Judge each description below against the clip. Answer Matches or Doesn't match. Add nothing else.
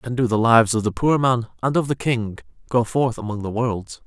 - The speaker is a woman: Doesn't match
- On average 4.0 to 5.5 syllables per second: Matches